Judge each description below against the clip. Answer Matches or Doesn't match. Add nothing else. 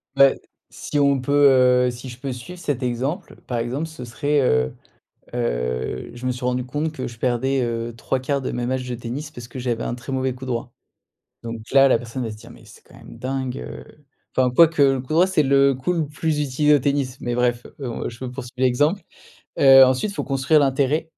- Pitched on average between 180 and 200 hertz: Doesn't match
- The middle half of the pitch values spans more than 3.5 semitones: Doesn't match